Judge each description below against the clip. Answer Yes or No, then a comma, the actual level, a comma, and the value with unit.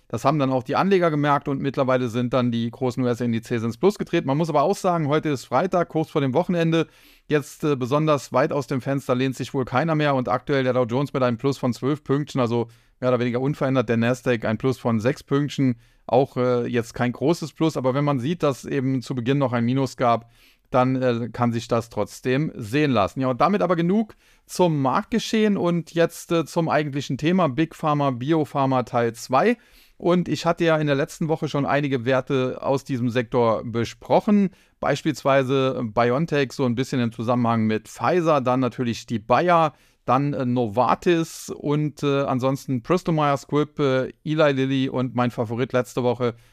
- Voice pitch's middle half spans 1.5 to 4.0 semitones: Yes, average, 3.3 semitones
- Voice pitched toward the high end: No, low, 135 Hz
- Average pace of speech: No, fast, 195 wpm